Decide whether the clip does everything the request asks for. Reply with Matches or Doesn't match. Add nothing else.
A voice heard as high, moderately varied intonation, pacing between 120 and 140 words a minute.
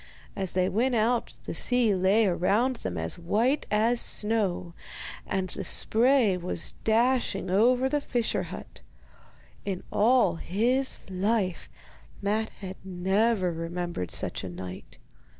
Matches